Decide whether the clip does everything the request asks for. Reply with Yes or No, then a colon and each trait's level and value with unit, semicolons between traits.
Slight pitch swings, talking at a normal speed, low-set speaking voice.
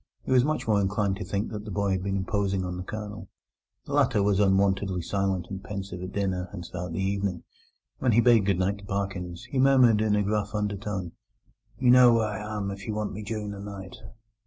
No: narrow, 1.7 semitones; fast, 220 wpm; low, 100 Hz